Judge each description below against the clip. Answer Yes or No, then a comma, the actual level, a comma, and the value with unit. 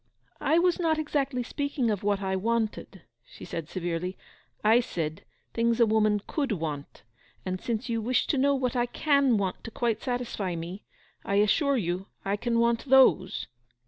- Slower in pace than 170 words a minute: No, average, 175 wpm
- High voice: Yes, high, 225 Hz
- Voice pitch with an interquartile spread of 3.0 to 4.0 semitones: No, average, 5.0 semitones